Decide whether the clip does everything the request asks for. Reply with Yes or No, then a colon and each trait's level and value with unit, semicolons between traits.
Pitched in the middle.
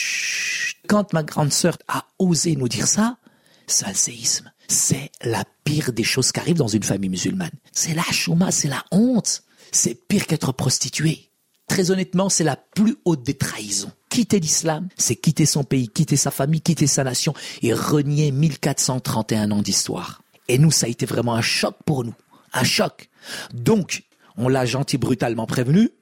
Yes: medium, 155 Hz